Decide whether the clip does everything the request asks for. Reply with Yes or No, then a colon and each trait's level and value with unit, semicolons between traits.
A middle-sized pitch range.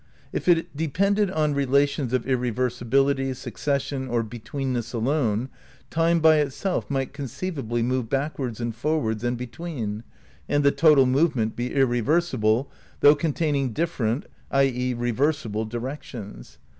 Yes: average, 3.7 semitones